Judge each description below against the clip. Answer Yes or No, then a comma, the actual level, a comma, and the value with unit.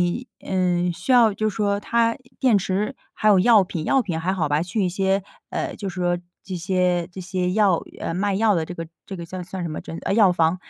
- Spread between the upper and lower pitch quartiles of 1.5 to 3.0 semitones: Yes, average, 2.7 semitones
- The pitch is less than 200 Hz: Yes, medium, 185 Hz